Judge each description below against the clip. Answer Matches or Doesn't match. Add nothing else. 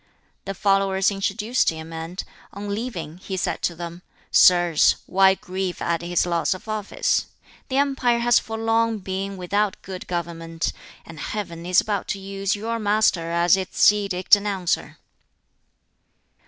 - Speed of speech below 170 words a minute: Matches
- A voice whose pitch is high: Matches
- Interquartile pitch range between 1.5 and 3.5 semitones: Matches